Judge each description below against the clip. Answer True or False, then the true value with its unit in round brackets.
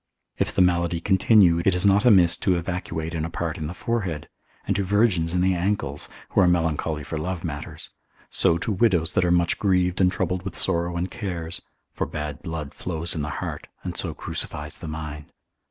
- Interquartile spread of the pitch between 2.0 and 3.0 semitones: True (2.4 semitones)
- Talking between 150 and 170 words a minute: False (200 wpm)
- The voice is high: False (85 Hz)